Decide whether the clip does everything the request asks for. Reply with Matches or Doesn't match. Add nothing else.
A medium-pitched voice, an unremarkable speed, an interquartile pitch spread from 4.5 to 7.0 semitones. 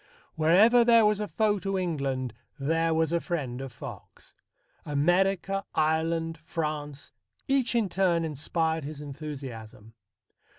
Doesn't match